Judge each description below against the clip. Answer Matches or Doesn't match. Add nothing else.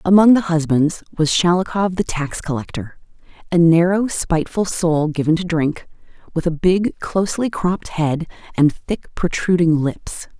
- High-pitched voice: Doesn't match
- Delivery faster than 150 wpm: Doesn't match